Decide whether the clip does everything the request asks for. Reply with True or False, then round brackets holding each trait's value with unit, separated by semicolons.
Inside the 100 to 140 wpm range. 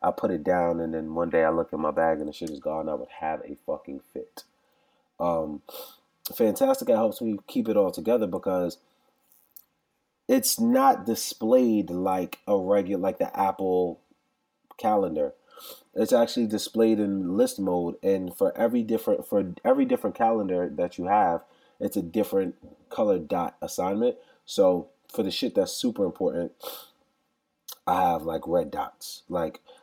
False (160 wpm)